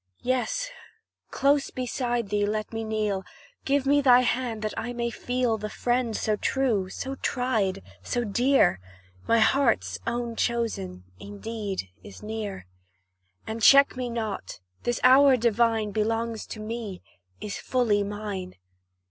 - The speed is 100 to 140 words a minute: Yes, slow, 135 wpm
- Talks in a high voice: Yes, high, 230 Hz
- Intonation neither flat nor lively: Yes, average, 3.1 semitones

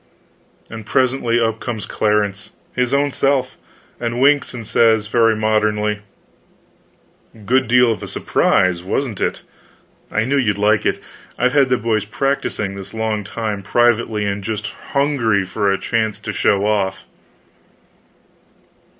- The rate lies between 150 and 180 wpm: No, average, 140 wpm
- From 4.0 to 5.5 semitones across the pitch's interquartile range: No, average, 3.0 semitones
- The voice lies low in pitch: Yes, low, 110 Hz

